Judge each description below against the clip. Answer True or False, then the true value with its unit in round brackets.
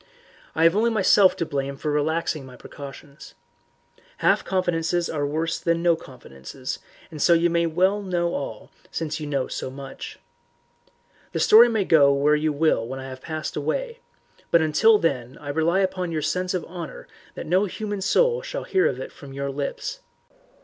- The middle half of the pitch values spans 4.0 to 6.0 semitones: True (4.5 semitones)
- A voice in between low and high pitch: True (165 Hz)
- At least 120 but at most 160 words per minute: False (175 wpm)